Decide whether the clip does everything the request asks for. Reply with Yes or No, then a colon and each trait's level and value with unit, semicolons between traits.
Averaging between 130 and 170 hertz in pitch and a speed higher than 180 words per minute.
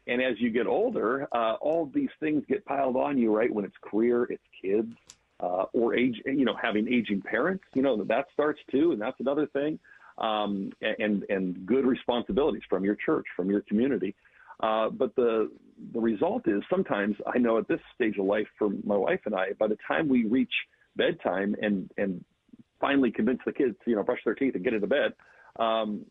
No: low, 120 Hz; average, 200 wpm